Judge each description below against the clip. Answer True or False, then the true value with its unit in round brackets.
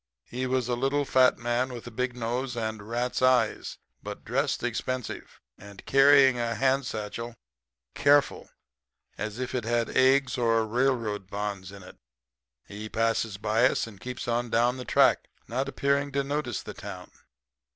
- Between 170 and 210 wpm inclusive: False (160 wpm)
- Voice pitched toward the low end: True (120 Hz)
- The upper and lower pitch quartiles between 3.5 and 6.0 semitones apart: False (2.9 semitones)